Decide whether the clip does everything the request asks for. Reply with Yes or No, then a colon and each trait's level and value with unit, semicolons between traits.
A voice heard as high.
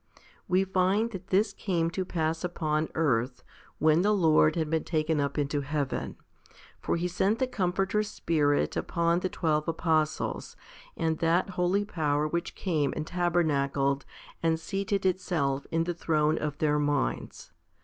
No: medium, 165 Hz